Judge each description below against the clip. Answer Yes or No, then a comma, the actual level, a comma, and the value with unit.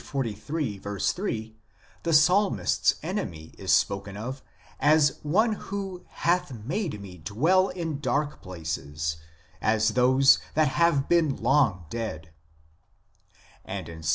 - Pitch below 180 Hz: Yes, low, 135 Hz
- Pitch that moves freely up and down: Yes, wide, 8.8 semitones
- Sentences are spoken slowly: Yes, slow, 115 wpm